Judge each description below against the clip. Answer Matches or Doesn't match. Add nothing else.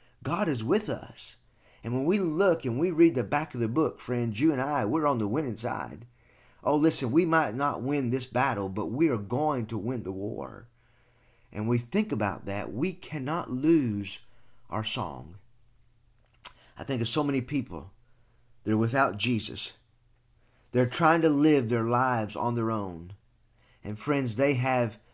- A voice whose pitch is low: Matches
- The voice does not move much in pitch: Doesn't match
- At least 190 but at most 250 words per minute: Doesn't match